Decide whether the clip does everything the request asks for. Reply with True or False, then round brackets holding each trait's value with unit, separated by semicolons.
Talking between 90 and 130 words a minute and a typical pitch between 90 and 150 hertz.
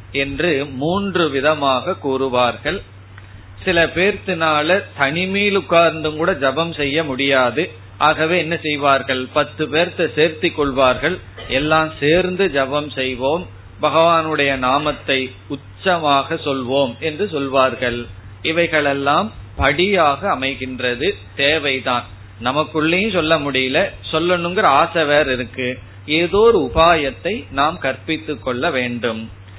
True (95 wpm; 140 Hz)